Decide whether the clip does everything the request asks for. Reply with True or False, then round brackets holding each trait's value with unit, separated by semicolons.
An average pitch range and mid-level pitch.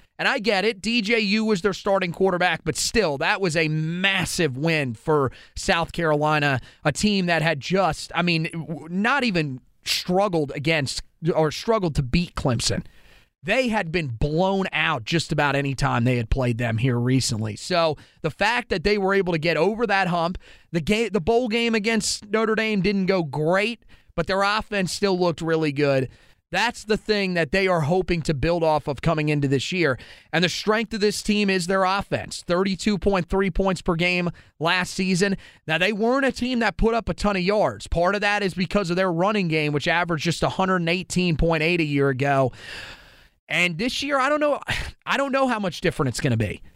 True (4.6 semitones; 175 Hz)